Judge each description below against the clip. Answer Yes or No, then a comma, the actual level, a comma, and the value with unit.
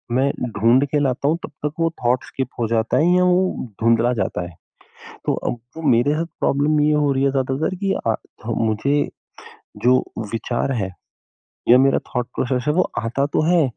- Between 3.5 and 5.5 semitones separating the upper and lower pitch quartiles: Yes, average, 4.0 semitones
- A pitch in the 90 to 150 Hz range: Yes, low, 135 Hz